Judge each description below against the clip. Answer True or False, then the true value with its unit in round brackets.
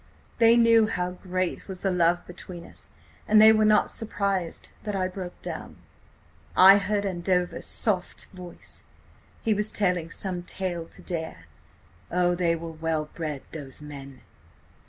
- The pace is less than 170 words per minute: True (150 wpm)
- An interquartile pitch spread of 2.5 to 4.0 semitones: True (3.0 semitones)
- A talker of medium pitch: True (180 Hz)